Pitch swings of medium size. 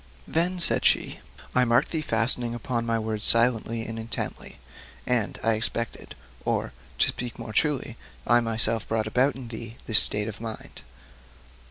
No: narrow, 1.7 semitones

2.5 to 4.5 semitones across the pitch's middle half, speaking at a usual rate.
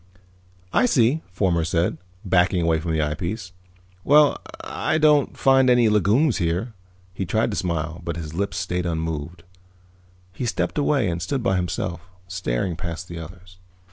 No: average, 5.2 semitones; average, 155 wpm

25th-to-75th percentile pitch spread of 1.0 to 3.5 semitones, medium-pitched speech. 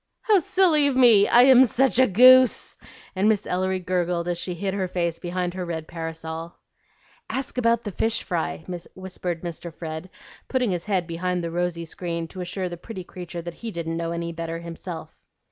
No: average, 4.2 semitones; medium, 180 Hz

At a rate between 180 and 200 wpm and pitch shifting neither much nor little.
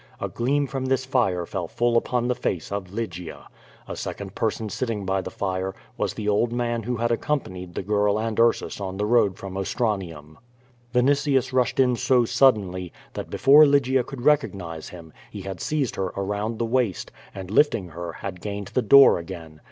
Yes: average, 185 wpm; average, 4.9 semitones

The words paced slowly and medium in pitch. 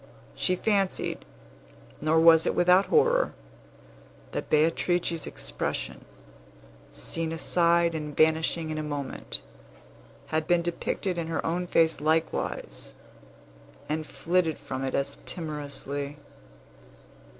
Yes: slow, 105 wpm; medium, 160 Hz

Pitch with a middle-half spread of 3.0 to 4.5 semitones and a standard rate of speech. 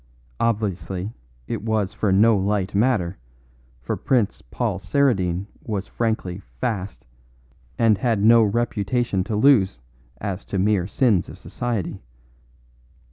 No: average, 3.3 semitones; slow, 125 wpm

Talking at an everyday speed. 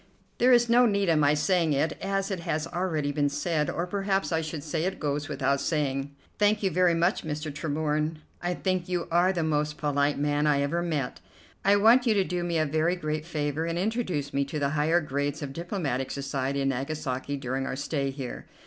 No: fast, 210 wpm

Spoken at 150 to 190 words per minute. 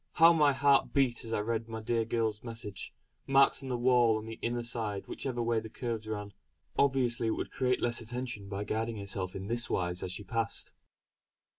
No: average, 200 wpm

